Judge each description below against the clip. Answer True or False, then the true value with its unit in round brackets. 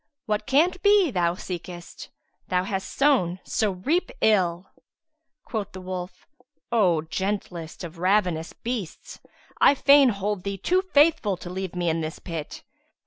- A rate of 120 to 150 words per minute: True (145 wpm)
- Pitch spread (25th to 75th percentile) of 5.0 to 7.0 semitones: True (5.5 semitones)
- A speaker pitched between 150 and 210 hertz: True (190 Hz)